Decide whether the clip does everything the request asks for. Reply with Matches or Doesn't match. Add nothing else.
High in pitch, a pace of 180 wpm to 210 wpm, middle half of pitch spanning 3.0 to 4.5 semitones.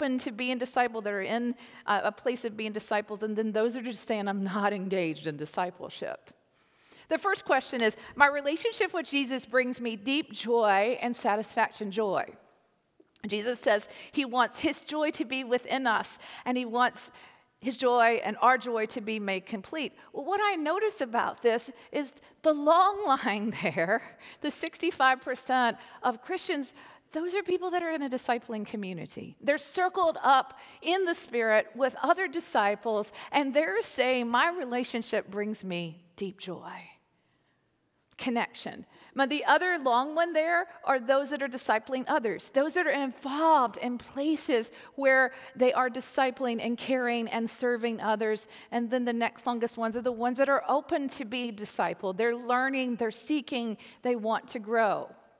Doesn't match